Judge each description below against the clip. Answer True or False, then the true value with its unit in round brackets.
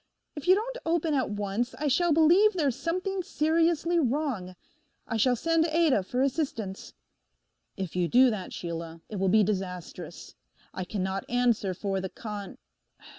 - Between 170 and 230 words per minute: False (155 wpm)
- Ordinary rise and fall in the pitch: False (9.0 semitones)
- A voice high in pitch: True (245 Hz)